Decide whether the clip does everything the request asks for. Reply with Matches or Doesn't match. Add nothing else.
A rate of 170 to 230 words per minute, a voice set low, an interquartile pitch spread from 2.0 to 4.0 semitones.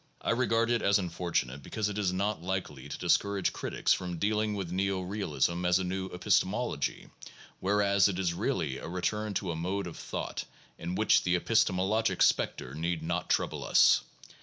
Matches